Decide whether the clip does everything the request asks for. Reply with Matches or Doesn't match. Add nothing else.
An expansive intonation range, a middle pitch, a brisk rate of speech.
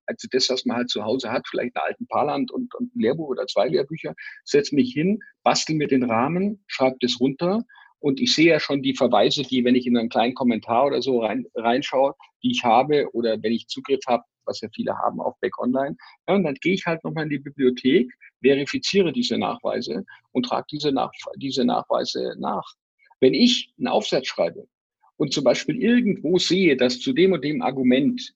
Matches